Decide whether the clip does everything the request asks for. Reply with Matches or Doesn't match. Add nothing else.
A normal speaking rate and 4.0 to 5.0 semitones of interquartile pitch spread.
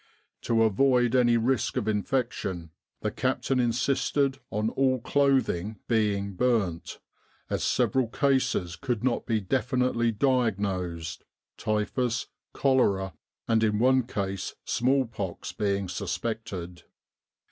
Doesn't match